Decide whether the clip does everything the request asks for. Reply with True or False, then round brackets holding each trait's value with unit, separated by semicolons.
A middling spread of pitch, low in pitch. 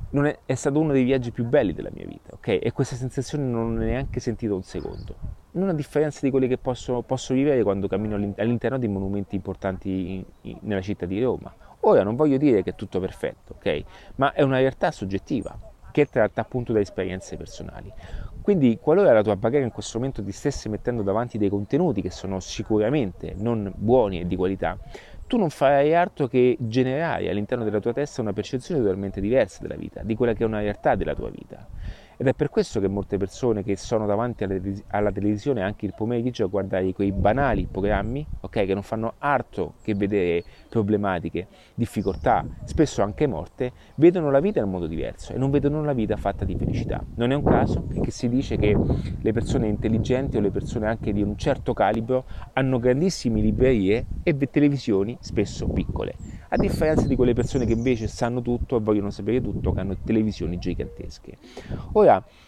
True (4.7 semitones; 110 Hz)